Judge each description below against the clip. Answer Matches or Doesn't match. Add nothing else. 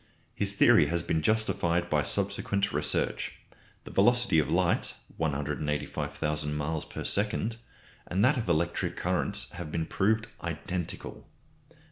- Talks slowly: Matches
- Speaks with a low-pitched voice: Matches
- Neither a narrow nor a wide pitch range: Matches